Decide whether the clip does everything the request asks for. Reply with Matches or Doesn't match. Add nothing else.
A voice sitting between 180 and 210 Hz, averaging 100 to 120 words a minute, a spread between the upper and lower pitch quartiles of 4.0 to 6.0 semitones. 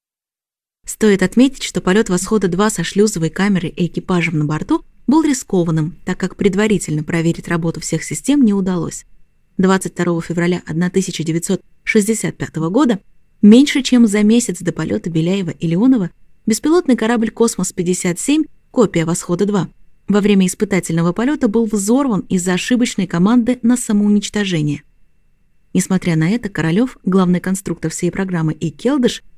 Doesn't match